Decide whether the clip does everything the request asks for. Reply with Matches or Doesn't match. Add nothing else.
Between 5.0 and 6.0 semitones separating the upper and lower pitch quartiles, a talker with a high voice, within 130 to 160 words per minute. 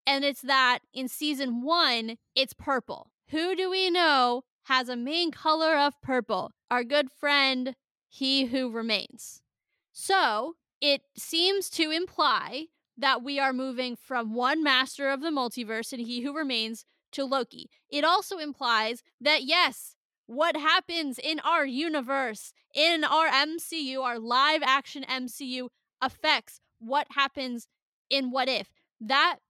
Doesn't match